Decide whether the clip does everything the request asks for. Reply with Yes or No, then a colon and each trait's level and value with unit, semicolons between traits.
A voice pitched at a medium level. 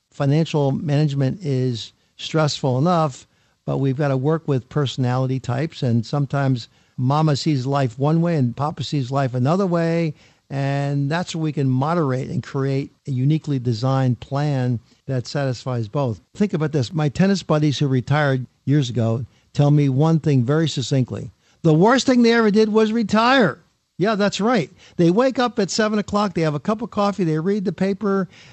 Yes: medium, 145 Hz